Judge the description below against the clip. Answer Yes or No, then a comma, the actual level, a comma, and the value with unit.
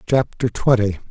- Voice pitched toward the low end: Yes, low, 120 Hz